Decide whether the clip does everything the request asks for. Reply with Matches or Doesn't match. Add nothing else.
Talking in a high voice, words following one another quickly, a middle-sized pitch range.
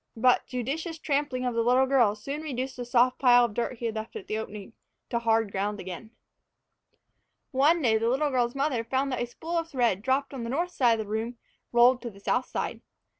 Matches